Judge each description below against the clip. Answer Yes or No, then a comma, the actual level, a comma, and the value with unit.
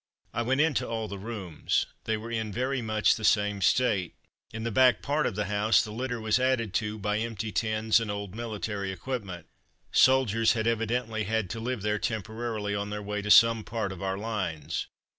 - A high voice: No, low, 110 Hz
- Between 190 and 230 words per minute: Yes, average, 200 wpm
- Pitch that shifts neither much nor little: No, narrow, 2.2 semitones